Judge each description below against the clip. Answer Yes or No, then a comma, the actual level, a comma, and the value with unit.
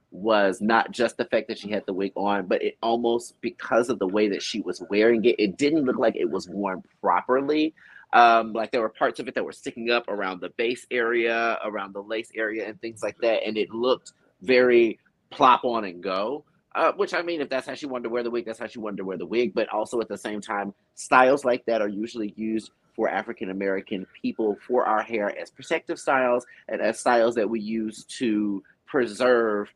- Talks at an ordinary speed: No, fast, 230 wpm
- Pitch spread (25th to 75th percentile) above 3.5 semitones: No, average, 2.7 semitones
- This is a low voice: Yes, low, 115 Hz